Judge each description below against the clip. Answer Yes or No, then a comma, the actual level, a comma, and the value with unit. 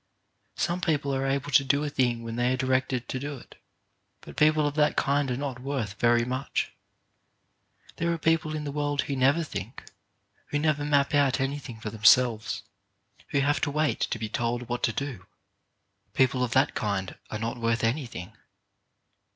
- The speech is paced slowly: No, average, 185 wpm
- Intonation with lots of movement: No, average, 3.4 semitones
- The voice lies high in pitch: No, low, 135 Hz